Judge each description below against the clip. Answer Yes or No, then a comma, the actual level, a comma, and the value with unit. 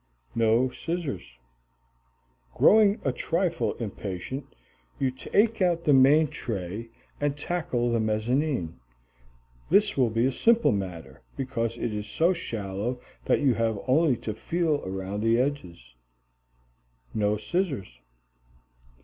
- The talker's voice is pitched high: No, low, 125 Hz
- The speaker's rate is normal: No, slow, 120 wpm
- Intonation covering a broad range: Yes, wide, 6.5 semitones